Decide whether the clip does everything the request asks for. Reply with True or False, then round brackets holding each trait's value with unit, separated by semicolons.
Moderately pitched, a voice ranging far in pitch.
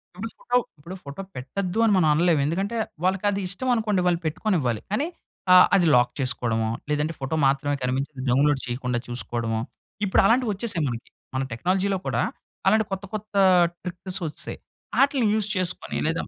True (175 Hz; 6.8 semitones)